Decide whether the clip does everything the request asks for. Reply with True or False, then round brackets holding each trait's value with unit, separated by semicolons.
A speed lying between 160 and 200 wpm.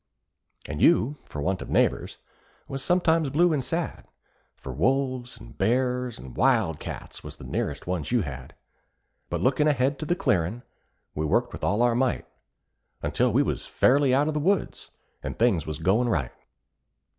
True (170 wpm)